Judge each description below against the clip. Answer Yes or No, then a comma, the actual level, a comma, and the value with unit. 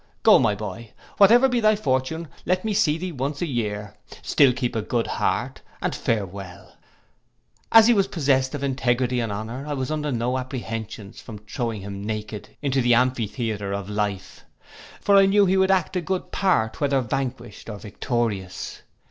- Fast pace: No, average, 175 wpm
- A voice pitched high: No, low, 125 Hz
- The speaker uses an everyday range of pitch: No, wide, 6.3 semitones